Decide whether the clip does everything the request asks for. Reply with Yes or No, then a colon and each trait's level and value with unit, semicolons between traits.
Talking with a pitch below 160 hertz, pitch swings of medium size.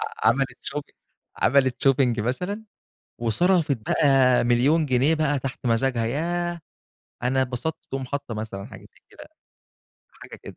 Yes: low, 135 Hz; average, 3.7 semitones